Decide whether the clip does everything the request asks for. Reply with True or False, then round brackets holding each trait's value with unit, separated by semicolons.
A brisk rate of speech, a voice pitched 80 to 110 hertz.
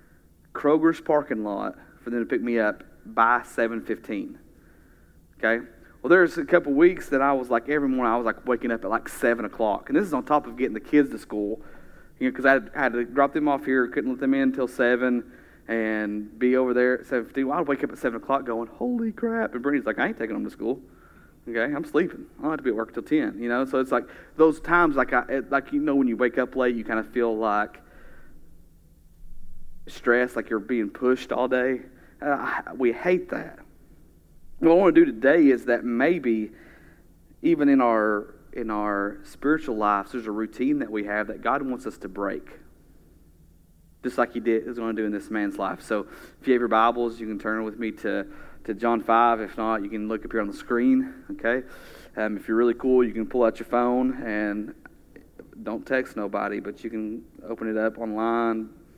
False (225 wpm; 120 Hz)